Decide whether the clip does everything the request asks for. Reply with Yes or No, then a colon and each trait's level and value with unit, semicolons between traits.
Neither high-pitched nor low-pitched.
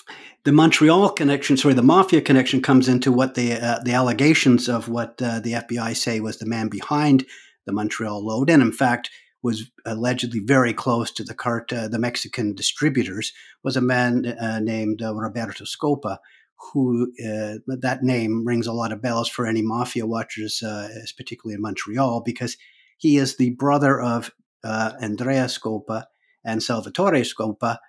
No: low, 120 Hz